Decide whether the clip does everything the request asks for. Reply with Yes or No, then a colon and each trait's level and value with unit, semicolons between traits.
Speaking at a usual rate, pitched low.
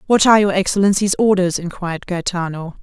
No: average, 150 wpm; medium, 185 Hz